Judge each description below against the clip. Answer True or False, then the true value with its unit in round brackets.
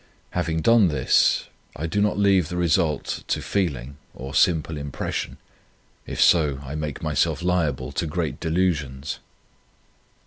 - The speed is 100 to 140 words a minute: True (135 wpm)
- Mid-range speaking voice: False (80 Hz)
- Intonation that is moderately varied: True (3.7 semitones)